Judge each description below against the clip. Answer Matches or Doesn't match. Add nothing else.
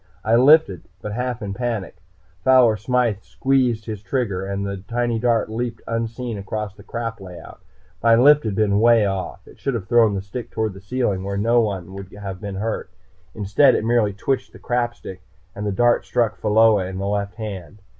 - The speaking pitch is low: Matches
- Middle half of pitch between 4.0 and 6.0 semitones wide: Doesn't match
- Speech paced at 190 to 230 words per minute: Matches